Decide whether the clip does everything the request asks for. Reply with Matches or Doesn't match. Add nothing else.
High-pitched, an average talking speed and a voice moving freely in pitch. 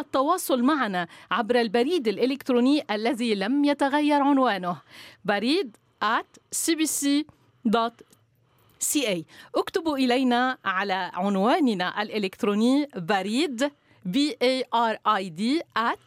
Matches